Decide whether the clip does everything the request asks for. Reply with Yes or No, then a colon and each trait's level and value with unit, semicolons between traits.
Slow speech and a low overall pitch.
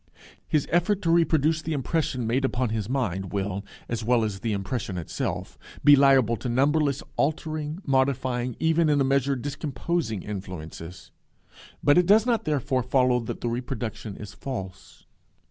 No: average, 155 wpm; low, 130 Hz